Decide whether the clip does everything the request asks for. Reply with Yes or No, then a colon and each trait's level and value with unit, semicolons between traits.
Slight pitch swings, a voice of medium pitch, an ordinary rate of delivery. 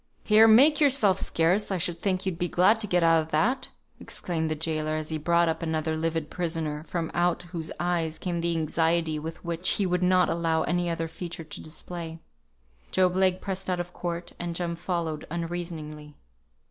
Yes: narrow, 1.9 semitones; medium, 170 Hz; average, 185 wpm